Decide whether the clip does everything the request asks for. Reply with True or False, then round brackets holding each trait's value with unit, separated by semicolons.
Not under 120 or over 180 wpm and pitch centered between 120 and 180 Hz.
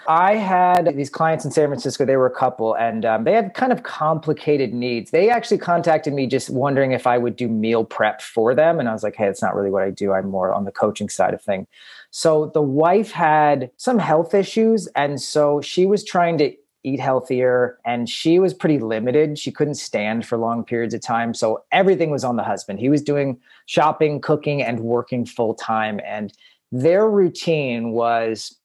False (205 wpm; 135 Hz)